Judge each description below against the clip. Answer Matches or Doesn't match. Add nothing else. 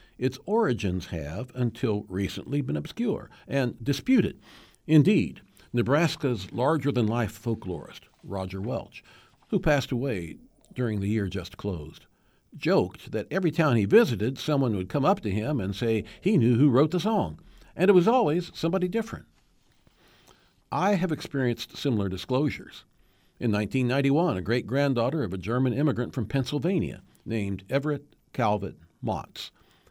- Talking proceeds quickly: Doesn't match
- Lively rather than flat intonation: Matches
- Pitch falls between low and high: Doesn't match